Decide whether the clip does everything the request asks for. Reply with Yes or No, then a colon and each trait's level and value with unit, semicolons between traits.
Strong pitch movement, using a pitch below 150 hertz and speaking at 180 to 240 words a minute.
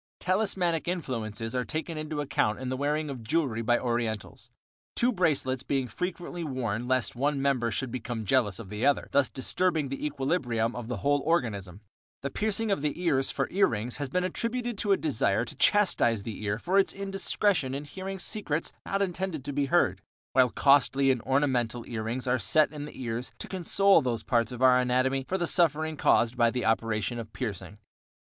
Yes: wide, 5.8 semitones; low, 135 Hz; average, 195 wpm